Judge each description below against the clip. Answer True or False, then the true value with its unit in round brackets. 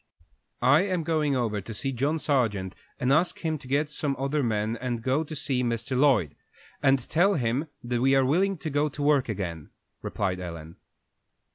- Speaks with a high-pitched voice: False (135 Hz)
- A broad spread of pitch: False (4.7 semitones)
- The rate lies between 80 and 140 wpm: False (180 wpm)